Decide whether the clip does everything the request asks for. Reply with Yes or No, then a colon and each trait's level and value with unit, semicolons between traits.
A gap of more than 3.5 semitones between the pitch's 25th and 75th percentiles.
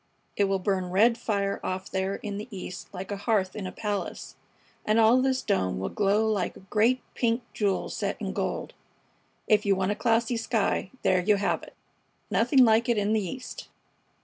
No: average, 2.8 semitones